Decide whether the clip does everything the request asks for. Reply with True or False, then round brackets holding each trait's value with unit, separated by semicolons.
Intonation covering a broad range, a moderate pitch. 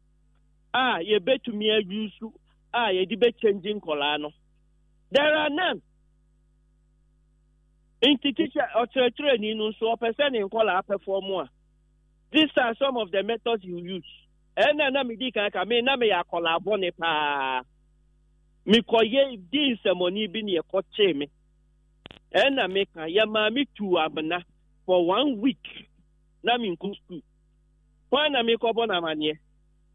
False (7.5 semitones; 195 Hz)